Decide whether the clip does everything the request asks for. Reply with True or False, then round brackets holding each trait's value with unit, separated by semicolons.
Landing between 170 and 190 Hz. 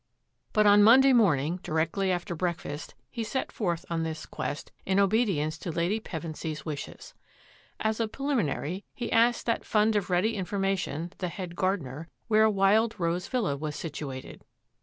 True (185 Hz)